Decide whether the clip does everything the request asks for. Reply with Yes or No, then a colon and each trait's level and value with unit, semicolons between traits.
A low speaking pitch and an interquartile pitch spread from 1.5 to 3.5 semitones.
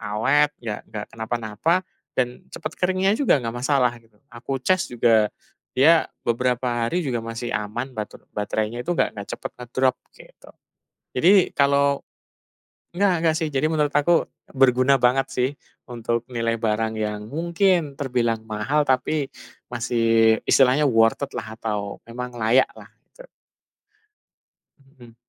No: low, 125 Hz; average, 4.0 semitones